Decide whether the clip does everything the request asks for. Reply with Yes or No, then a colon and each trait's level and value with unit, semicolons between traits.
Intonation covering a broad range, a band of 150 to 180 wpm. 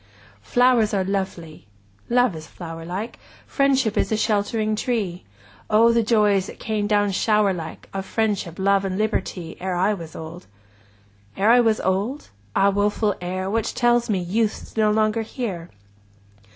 No: average, 3.0 semitones; average, 165 wpm